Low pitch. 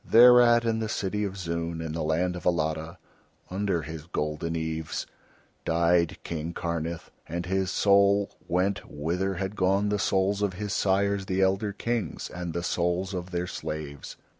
Yes: very low, 90 Hz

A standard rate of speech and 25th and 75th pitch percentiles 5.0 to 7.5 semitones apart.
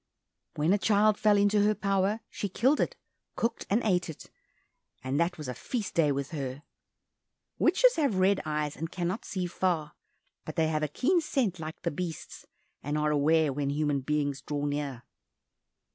Yes: average, 175 wpm; wide, 5.5 semitones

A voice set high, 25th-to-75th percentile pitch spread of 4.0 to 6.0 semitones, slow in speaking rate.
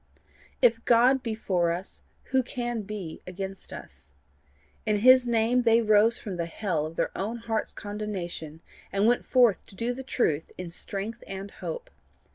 No: high, 210 Hz; average, 4.4 semitones; average, 165 wpm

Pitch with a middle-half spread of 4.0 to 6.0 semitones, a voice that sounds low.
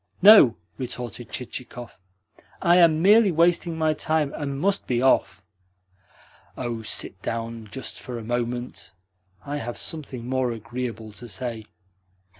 Yes: average, 5.1 semitones; low, 125 Hz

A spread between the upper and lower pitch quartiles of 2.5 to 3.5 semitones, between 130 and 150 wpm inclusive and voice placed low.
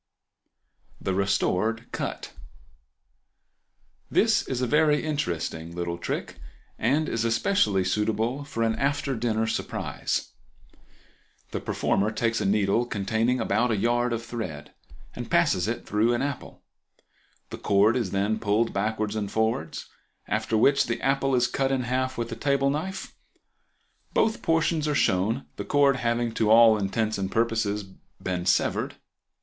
No: average, 4.1 semitones; average, 140 wpm; low, 115 Hz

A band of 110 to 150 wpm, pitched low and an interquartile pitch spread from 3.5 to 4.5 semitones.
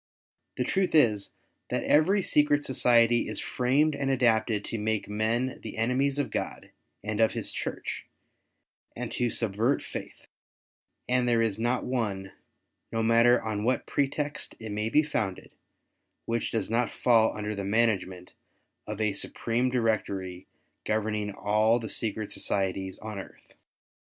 No: average, 145 wpm; low, 115 Hz; average, 2.9 semitones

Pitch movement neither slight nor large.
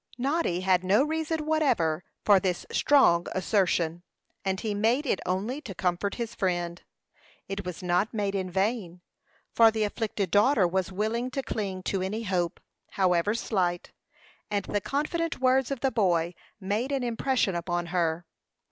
Yes: average, 4.9 semitones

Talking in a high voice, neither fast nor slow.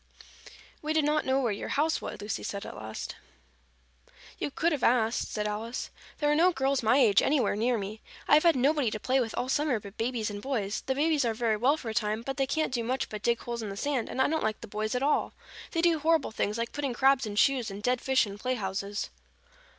No: high, 245 Hz; fast, 245 wpm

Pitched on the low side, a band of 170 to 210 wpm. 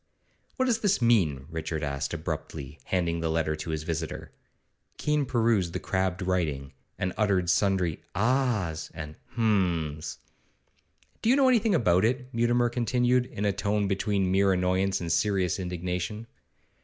No: very low, 95 Hz; average, 145 wpm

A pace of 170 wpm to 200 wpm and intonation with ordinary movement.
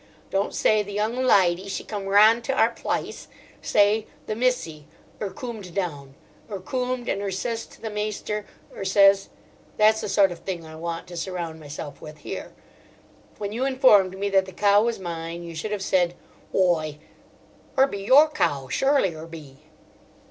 Yes: average, 180 wpm; average, 4.1 semitones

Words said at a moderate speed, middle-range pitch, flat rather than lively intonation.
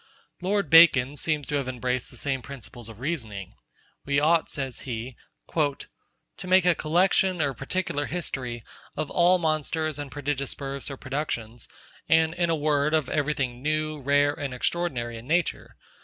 No: average, 160 wpm; medium, 145 Hz; average, 3.7 semitones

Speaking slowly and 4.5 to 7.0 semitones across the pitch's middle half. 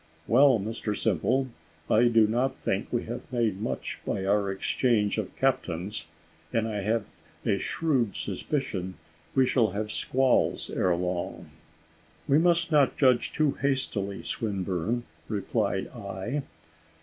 Yes: slow, 130 wpm; average, 4.8 semitones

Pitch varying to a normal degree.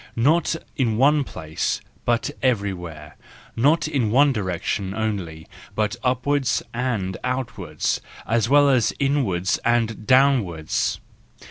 No: wide, 5.7 semitones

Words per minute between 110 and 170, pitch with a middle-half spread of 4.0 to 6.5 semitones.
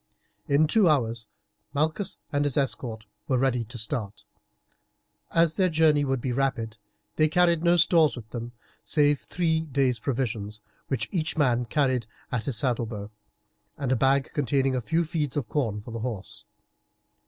Yes: average, 160 wpm; average, 4.8 semitones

